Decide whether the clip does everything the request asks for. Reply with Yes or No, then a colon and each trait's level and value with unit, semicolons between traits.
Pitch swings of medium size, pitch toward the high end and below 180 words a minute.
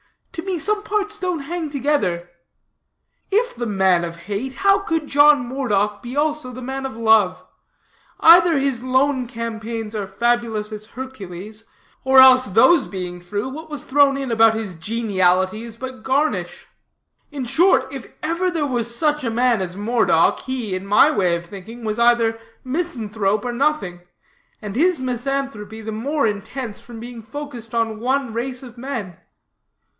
Yes: average, 4.7 semitones; high, 240 Hz; average, 160 wpm